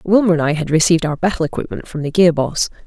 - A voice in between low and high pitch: Yes, medium, 165 Hz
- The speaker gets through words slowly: No, fast, 250 wpm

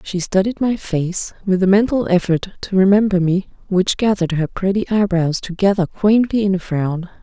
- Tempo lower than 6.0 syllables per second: Yes, 5.1 syllables/s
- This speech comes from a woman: Yes, female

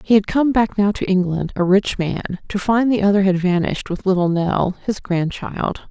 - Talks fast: Yes, fast, 215 wpm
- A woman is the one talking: Yes, female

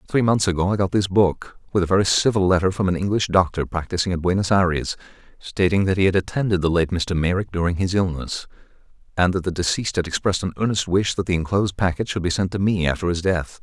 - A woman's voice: No, male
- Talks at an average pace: No, fast, 235 wpm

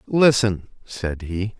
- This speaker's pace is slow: Yes, slow, 115 wpm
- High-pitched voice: No, low, 105 Hz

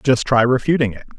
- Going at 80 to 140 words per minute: No, average, 200 wpm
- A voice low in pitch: Yes, low, 125 Hz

